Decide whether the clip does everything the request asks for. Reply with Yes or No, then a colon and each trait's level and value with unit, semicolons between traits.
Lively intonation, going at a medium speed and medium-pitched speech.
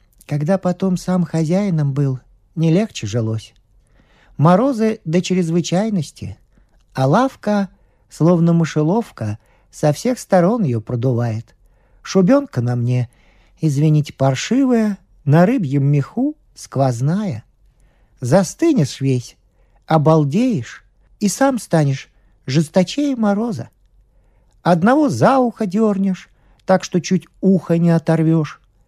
No: wide, 7.9 semitones; slow, 100 wpm; medium, 160 Hz